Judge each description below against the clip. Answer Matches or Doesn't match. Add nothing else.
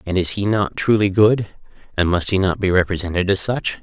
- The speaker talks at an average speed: Doesn't match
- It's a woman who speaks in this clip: Doesn't match